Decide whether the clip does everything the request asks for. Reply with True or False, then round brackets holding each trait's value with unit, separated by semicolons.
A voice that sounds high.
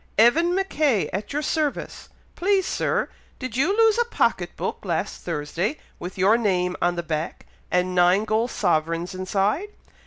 True (210 Hz)